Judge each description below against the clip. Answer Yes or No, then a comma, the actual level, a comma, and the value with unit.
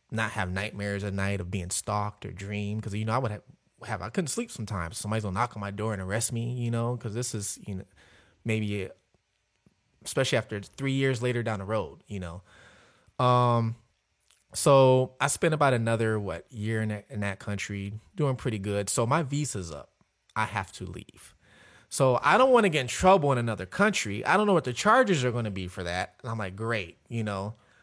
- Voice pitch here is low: Yes, low, 110 Hz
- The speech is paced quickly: Yes, fast, 220 wpm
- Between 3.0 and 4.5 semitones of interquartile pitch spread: Yes, average, 3.7 semitones